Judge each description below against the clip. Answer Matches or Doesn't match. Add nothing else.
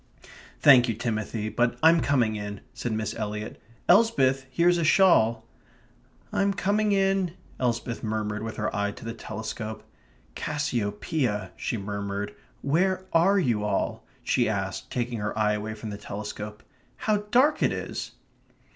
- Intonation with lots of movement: Matches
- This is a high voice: Doesn't match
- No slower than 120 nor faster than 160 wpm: Matches